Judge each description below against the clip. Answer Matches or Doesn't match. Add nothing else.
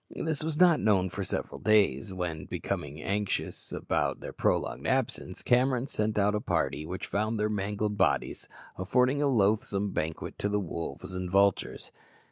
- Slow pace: Doesn't match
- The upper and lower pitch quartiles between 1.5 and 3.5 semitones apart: Matches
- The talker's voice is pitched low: Matches